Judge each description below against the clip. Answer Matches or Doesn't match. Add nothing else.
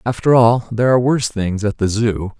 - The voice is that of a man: Matches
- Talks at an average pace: Doesn't match